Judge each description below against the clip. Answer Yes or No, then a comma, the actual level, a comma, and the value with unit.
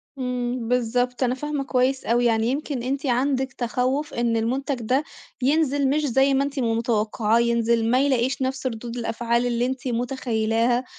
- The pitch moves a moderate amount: No, narrow, 2.2 semitones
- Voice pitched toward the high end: Yes, very high, 250 Hz